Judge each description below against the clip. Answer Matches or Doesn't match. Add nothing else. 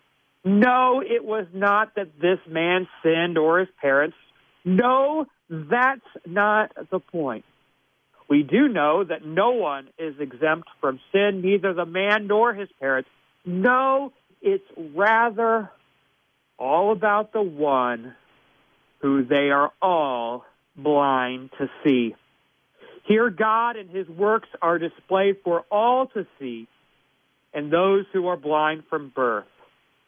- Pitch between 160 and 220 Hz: Matches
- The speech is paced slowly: Matches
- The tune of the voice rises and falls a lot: Matches